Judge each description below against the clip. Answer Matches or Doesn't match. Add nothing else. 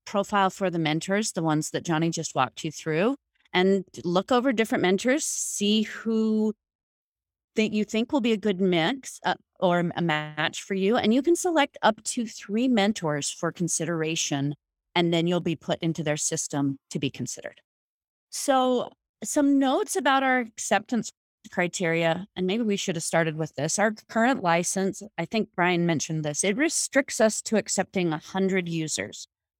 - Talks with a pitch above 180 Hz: Matches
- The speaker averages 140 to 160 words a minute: Doesn't match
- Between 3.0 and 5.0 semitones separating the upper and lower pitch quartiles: Doesn't match